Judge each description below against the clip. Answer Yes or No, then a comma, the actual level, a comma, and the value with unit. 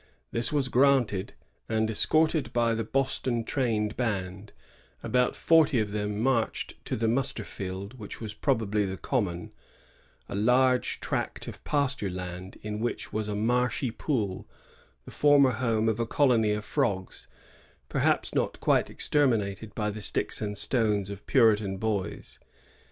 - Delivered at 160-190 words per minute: No, average, 150 wpm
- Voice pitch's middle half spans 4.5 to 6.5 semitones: No, average, 3.6 semitones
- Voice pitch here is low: Yes, low, 110 Hz